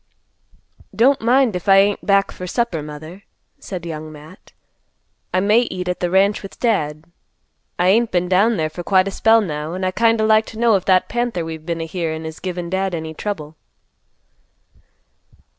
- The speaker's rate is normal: Yes, average, 190 wpm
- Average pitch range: Yes, average, 4.5 semitones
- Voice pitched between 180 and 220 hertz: Yes, medium, 185 Hz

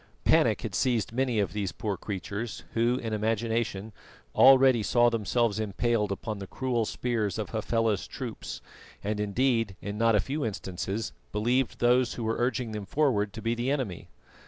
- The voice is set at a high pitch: No, low, 115 Hz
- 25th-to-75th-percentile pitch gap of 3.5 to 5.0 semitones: No, narrow, 2.6 semitones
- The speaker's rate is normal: Yes, average, 165 wpm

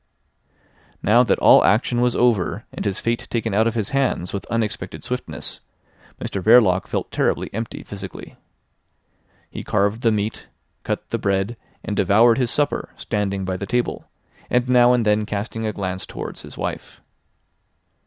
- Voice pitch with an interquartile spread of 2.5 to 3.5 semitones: Yes, average, 3.0 semitones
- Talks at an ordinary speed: Yes, average, 160 wpm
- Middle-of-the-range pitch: No, low, 110 Hz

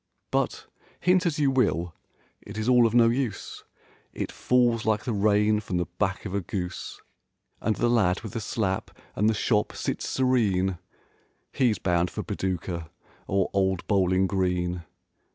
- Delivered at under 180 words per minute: Yes, average, 160 wpm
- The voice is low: Yes, low, 100 Hz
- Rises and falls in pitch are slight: No, average, 4.0 semitones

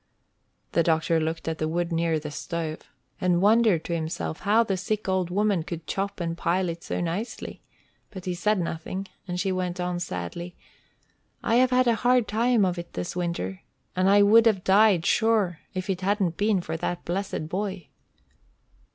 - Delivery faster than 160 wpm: Yes, average, 185 wpm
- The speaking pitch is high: No, medium, 180 Hz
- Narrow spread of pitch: No, average, 3.4 semitones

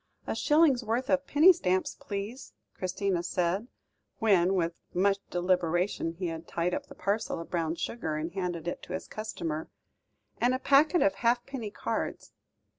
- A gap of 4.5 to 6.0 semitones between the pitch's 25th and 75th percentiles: Yes, wide, 5.4 semitones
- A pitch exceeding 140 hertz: Yes, high, 190 Hz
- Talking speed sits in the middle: Yes, average, 155 wpm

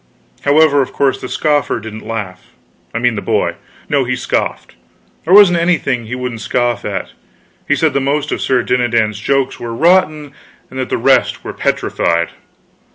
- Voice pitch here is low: Yes, low, 130 Hz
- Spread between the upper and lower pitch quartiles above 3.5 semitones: Yes, average, 3.9 semitones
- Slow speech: No, average, 165 wpm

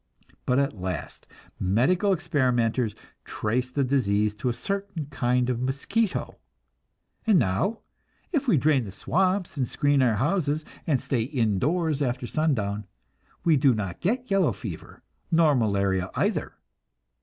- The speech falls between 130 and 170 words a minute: Yes, average, 140 wpm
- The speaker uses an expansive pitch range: Yes, wide, 6.5 semitones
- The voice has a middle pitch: No, low, 130 Hz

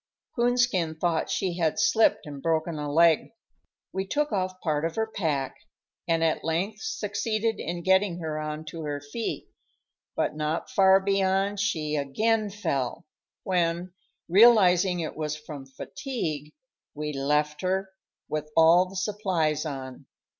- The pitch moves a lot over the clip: No, average, 4.3 semitones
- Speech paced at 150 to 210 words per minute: No, average, 140 wpm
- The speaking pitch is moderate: Yes, medium, 170 Hz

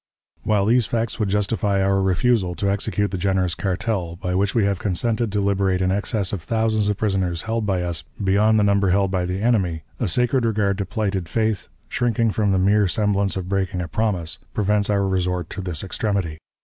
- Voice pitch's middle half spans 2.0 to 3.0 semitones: Yes, narrow, 2.4 semitones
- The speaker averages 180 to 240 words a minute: Yes, average, 200 wpm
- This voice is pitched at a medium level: No, low, 100 Hz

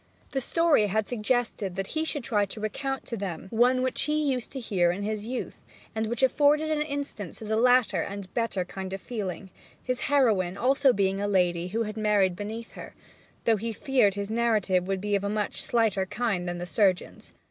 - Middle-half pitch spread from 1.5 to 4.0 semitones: No, average, 4.4 semitones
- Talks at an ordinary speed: No, fast, 210 wpm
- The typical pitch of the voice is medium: No, high, 215 Hz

